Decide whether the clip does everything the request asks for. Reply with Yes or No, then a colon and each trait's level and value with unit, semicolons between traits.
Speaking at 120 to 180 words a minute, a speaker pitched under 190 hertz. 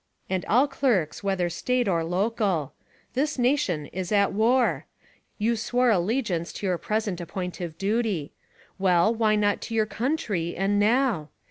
No: average, 150 wpm; high, 205 Hz